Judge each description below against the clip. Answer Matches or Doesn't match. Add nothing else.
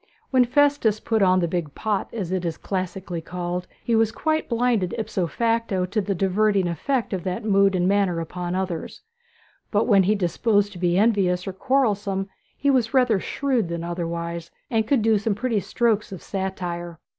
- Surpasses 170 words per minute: Matches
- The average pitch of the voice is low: Doesn't match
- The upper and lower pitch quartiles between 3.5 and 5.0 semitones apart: Matches